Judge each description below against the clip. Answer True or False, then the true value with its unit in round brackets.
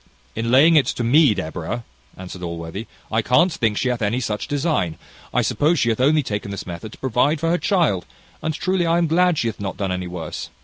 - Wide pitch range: True (7.9 semitones)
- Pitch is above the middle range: False (120 Hz)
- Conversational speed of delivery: False (220 wpm)